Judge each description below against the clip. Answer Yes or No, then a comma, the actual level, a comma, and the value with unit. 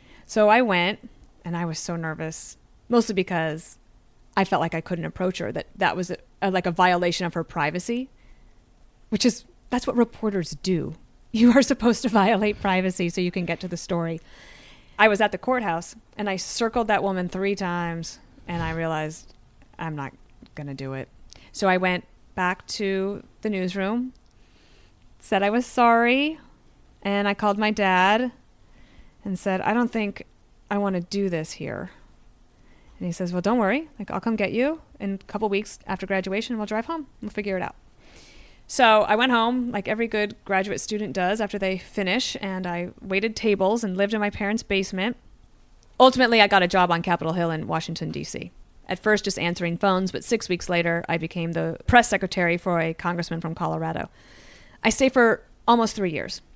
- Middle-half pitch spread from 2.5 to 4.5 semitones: Yes, average, 3.8 semitones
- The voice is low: No, high, 195 Hz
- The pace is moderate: Yes, average, 190 wpm